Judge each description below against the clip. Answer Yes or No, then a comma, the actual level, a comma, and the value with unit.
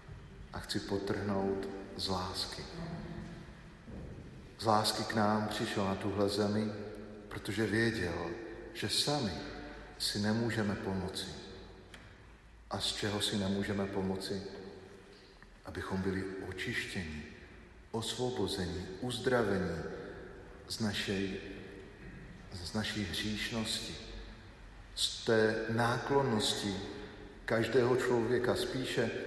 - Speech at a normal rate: No, slow, 85 wpm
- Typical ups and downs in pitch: No, narrow, 2.0 semitones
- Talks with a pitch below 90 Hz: No, low, 100 Hz